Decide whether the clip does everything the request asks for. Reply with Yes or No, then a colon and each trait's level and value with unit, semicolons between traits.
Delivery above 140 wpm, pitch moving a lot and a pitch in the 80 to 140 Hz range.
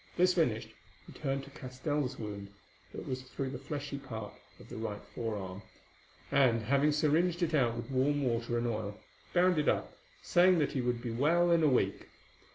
No: average, 185 wpm; average, 4.4 semitones; low, 135 Hz